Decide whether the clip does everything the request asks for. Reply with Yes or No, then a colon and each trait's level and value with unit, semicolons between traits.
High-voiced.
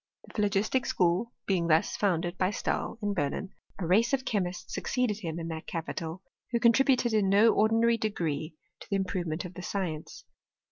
Yes: high, 195 Hz